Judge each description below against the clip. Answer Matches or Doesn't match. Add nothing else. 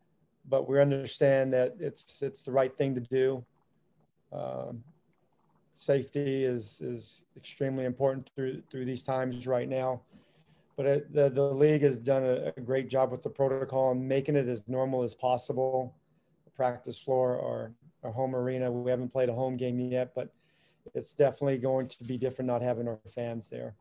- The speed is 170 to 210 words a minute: Matches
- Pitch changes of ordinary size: Doesn't match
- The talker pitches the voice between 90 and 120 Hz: Doesn't match